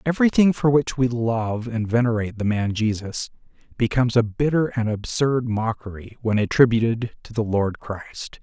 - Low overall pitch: Yes, low, 115 Hz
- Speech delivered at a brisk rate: No, average, 155 wpm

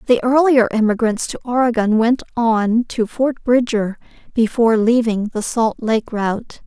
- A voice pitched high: Yes, high, 230 Hz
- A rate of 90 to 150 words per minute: Yes, average, 145 wpm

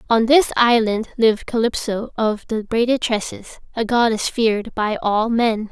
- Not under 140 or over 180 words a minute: Yes, average, 155 wpm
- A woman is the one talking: Yes, female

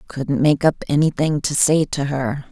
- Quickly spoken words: No, average, 190 wpm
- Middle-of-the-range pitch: Yes, medium, 145 Hz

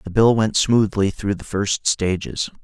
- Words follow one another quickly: No, average, 185 wpm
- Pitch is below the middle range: Yes, low, 105 Hz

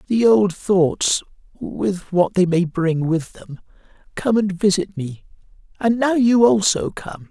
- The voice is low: No, high, 190 Hz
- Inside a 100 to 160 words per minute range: Yes, average, 155 wpm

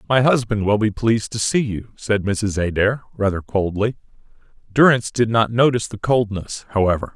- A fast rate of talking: No, average, 170 wpm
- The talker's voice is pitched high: No, low, 110 Hz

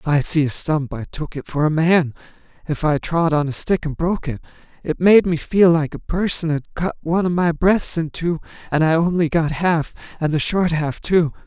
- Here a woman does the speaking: No, male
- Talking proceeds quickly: Yes, fast, 235 wpm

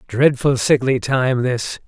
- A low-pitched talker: Yes, low, 130 Hz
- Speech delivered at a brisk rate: No, slow, 130 wpm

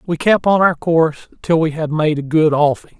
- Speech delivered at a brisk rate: Yes, fast, 240 wpm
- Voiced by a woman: No, male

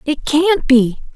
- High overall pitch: Yes, very high, 290 Hz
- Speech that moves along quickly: No, average, 155 wpm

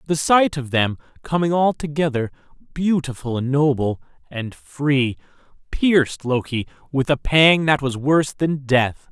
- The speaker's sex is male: Yes, male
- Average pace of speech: No, slow, 130 wpm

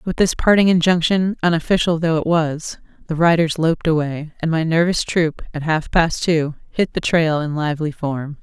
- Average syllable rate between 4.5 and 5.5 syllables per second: Yes, 5.0 syllables/s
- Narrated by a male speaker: No, female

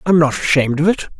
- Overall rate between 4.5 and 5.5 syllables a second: No, 7.1 syllables/s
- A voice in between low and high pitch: Yes, medium, 155 Hz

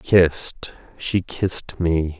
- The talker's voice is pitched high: No, very low, 85 Hz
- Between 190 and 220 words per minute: No, slow, 110 wpm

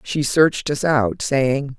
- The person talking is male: No, female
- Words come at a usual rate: Yes, average, 170 wpm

